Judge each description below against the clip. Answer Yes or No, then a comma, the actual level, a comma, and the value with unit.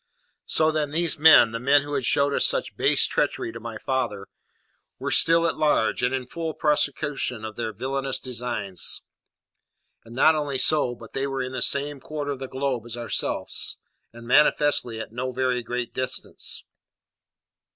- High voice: No, low, 130 Hz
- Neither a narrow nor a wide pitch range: Yes, average, 3.5 semitones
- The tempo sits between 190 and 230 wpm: No, average, 170 wpm